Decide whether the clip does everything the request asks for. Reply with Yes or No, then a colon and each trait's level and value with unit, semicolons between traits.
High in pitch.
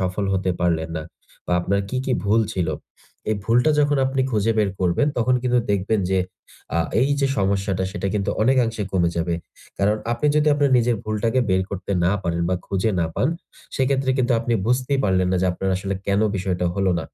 No: low, 100 Hz